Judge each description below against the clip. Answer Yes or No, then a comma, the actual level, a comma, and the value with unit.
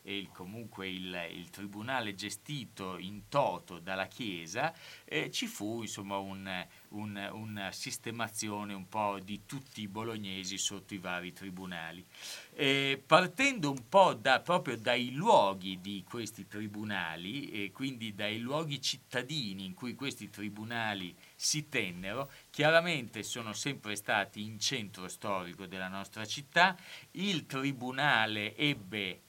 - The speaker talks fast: No, average, 130 wpm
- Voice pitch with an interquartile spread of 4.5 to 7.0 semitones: Yes, wide, 5.6 semitones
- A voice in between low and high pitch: No, low, 105 Hz